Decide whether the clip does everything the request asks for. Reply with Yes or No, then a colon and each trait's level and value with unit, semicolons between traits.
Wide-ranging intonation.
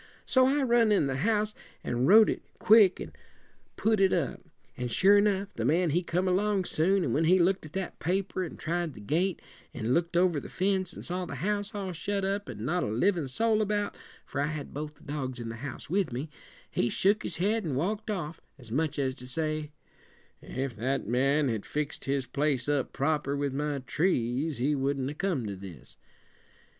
Yes: wide, 6.2 semitones